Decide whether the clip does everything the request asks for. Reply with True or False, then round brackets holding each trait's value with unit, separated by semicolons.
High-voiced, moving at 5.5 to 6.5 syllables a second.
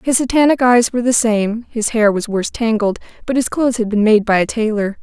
True (225 Hz; 5.8 syllables/s)